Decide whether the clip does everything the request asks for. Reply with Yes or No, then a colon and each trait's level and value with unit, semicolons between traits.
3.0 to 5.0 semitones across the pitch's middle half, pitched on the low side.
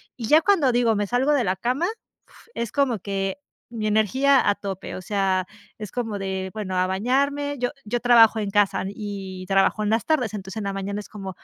No: average, 4.1 semitones; high, 210 Hz